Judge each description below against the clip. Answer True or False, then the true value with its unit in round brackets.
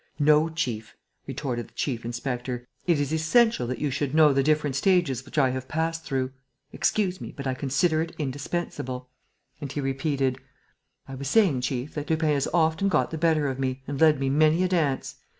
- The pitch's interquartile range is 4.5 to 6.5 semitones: False (3.5 semitones)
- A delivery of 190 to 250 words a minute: True (195 wpm)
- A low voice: False (145 Hz)